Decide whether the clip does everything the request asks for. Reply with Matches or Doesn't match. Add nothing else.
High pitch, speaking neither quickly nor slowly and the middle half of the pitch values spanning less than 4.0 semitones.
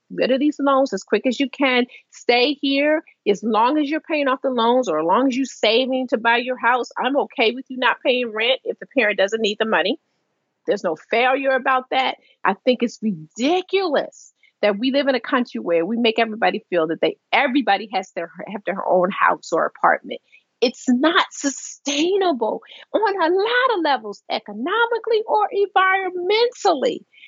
Doesn't match